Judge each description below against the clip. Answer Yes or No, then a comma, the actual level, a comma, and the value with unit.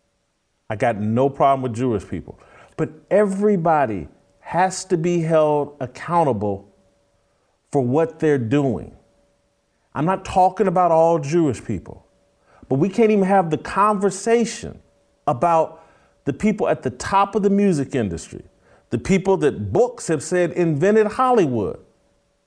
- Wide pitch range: Yes, wide, 8.0 semitones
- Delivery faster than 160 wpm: No, slow, 135 wpm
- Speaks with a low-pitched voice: No, medium, 160 Hz